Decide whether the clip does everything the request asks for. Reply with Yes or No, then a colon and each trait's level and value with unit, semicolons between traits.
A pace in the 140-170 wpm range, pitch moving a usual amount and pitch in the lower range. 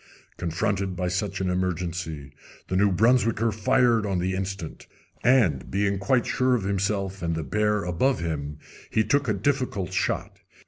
Yes: average, 155 wpm; average, 3.7 semitones; very low, 95 Hz